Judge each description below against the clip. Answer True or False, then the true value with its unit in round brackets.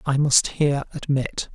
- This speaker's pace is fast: False (155 wpm)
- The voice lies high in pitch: False (140 Hz)